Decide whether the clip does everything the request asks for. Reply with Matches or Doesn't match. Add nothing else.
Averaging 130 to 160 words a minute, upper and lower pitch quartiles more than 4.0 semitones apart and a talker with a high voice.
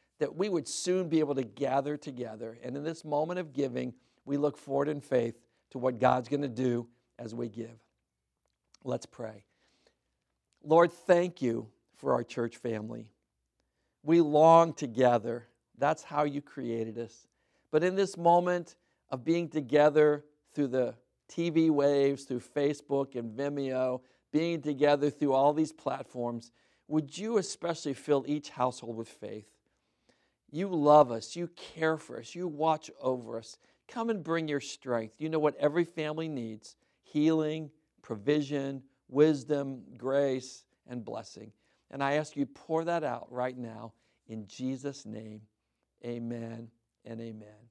Doesn't match